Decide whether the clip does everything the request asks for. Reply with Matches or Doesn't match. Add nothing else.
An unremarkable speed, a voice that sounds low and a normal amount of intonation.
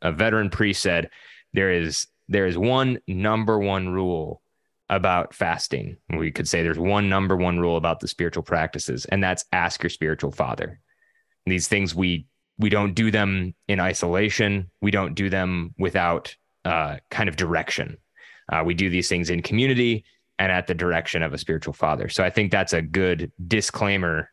Matches